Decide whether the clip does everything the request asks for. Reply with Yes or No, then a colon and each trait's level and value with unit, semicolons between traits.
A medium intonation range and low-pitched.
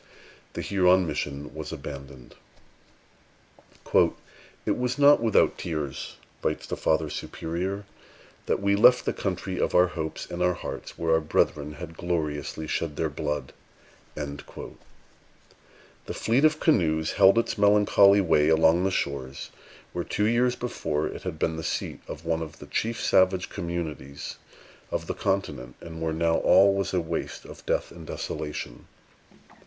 Yes: average, 4.4 semitones; very low, 85 Hz